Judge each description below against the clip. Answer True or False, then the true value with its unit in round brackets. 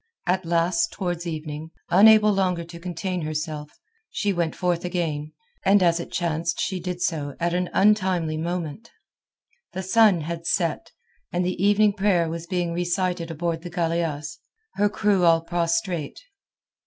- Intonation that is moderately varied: False (2.2 semitones)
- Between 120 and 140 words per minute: False (150 wpm)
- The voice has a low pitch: False (175 Hz)